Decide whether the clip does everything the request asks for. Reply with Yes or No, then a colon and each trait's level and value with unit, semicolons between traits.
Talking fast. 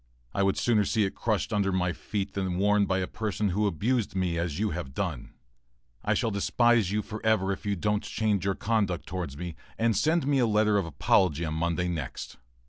Yes: fast, 215 wpm